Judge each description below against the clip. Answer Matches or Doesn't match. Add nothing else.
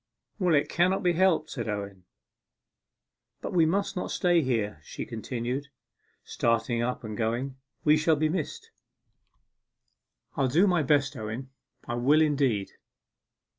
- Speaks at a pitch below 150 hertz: Matches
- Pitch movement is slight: Doesn't match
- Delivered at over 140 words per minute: Doesn't match